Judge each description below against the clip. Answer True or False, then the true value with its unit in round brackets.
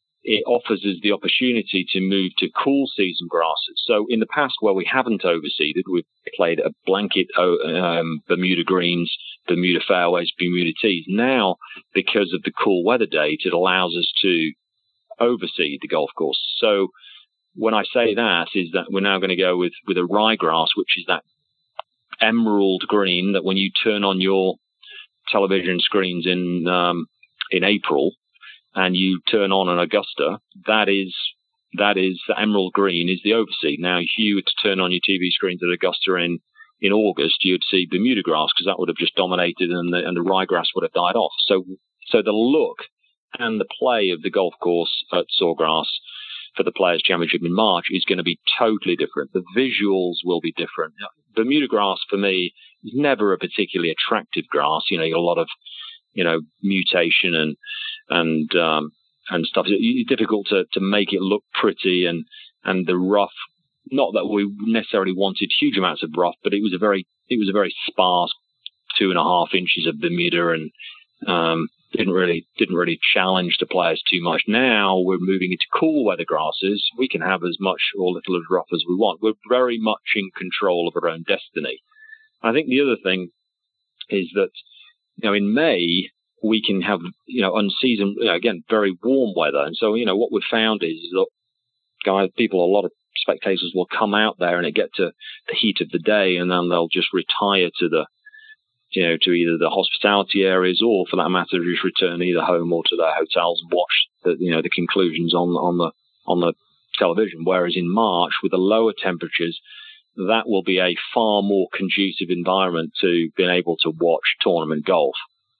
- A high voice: False (95 Hz)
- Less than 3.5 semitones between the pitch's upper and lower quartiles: False (3.8 semitones)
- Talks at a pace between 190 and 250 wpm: True (195 wpm)